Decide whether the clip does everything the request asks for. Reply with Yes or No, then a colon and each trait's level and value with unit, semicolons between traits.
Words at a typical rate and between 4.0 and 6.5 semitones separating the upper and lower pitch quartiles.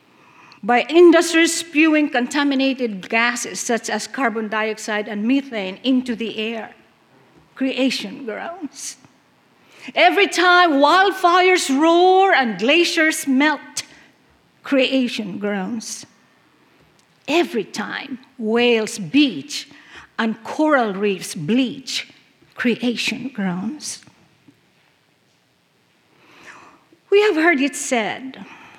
No: slow, 85 wpm; average, 5.2 semitones